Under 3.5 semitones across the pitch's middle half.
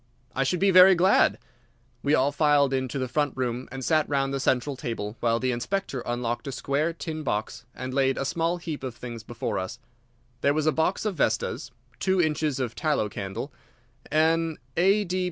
No: average, 4.3 semitones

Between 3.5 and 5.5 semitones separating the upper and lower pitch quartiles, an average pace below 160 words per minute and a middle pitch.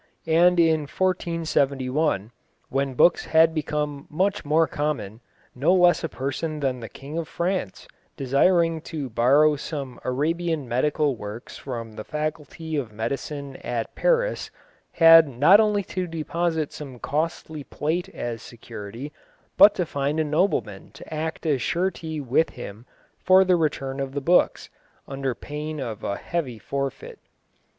Yes: average, 3.8 semitones; average, 145 wpm; medium, 150 Hz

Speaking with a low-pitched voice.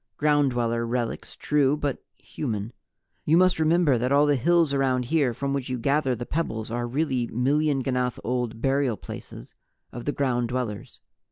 Yes: low, 130 Hz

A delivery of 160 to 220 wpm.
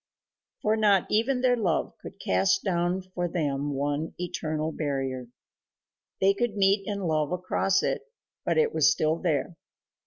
No: average, 150 wpm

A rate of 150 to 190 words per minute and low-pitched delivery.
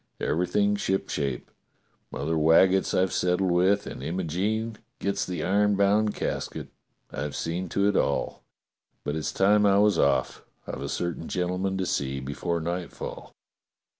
No: average, 140 wpm; very low, 90 Hz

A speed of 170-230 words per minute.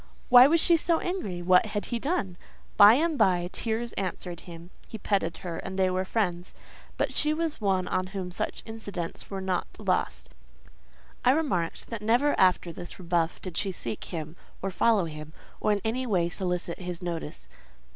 Yes: average, 180 wpm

